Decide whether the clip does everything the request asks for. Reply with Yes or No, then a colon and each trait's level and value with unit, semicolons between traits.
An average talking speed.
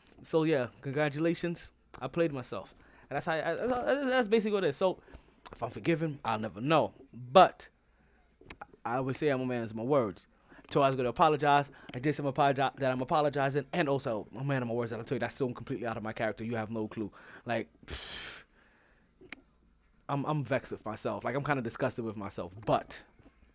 No: fast, 210 wpm